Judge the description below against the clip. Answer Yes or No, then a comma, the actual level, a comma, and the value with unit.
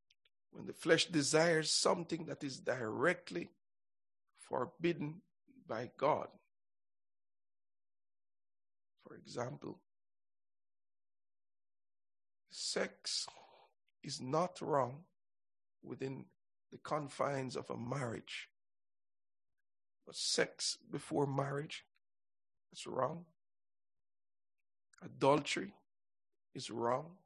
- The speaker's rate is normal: No, slow, 70 wpm